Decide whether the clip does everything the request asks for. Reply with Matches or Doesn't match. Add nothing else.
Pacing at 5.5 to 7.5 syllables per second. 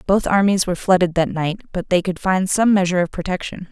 Matches